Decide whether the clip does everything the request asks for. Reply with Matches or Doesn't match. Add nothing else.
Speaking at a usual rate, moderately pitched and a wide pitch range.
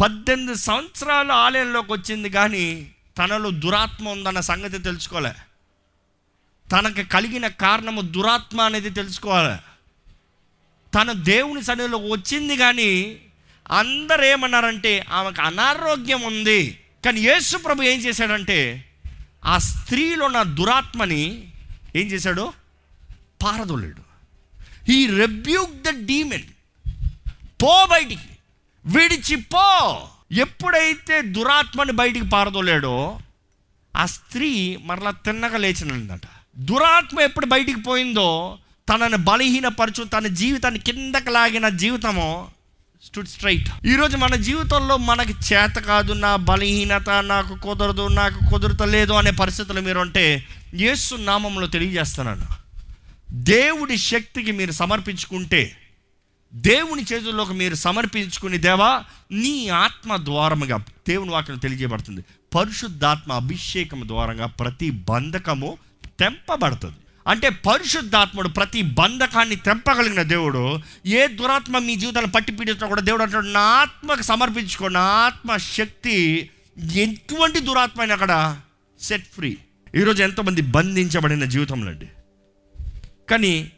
Doesn't match